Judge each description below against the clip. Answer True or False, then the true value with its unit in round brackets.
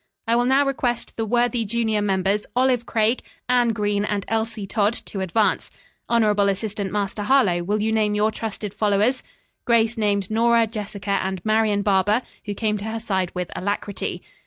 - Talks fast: False (170 wpm)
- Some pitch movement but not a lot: False (2.2 semitones)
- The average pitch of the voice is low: False (215 Hz)